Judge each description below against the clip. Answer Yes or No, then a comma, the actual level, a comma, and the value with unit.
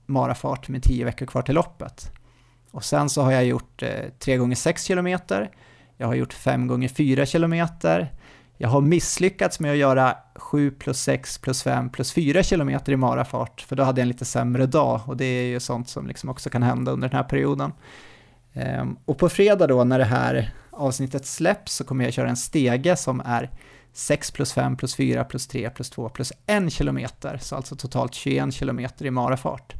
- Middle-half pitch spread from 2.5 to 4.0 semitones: Yes, average, 2.8 semitones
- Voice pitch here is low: Yes, low, 130 Hz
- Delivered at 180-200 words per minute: Yes, average, 190 wpm